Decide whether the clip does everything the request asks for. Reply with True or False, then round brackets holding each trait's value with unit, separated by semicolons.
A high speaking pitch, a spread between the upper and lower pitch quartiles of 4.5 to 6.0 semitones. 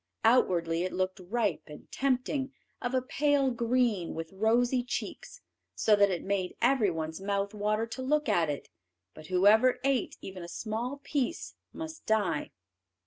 True (220 Hz; 5.6 semitones)